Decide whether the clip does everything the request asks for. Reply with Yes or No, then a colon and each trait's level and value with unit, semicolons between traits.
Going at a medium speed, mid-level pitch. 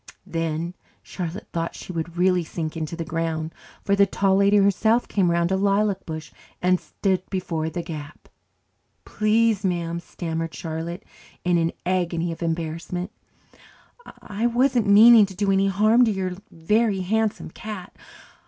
Yes: average, 150 wpm; medium, 180 Hz